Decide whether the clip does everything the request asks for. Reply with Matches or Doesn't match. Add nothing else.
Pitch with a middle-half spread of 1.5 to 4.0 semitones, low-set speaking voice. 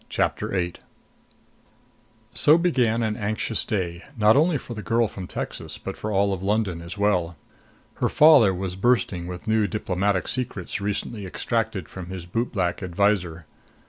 Matches